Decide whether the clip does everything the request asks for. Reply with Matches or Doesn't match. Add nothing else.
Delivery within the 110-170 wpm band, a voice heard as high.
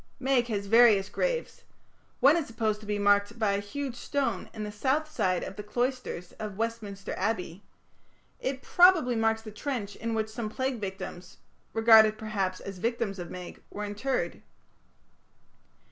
Matches